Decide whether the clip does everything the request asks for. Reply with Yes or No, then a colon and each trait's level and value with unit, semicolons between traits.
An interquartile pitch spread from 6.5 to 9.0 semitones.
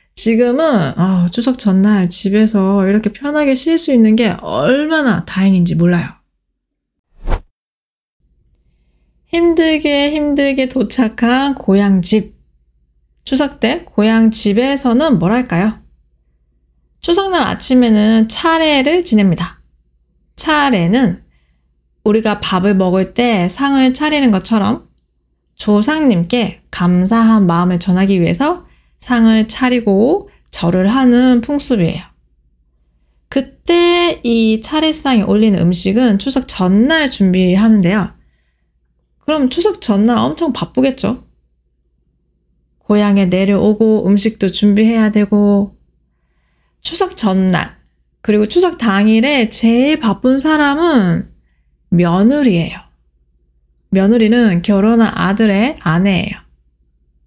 Yes: wide, 6.8 semitones